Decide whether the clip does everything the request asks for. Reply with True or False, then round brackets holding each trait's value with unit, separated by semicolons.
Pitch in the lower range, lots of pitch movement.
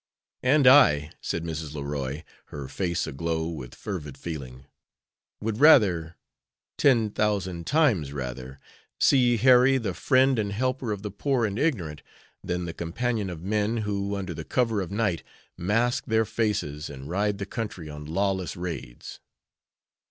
True (95 Hz; 6.3 semitones)